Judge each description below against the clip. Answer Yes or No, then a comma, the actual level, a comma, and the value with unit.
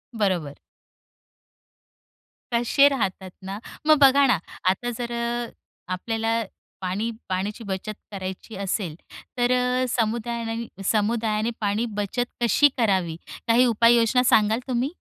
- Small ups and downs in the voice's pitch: No, average, 3.3 semitones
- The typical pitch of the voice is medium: No, high, 225 Hz